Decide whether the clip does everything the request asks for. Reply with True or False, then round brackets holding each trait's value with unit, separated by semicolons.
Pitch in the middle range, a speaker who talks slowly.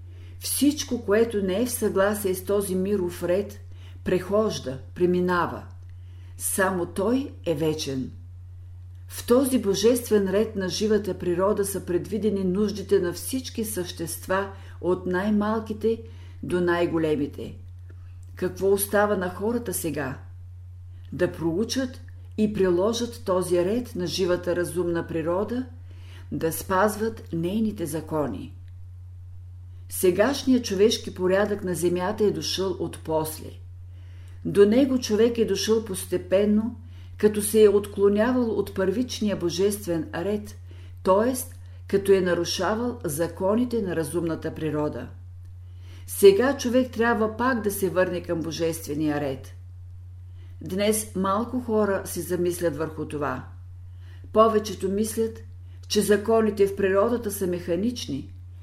True (175 Hz; 110 wpm)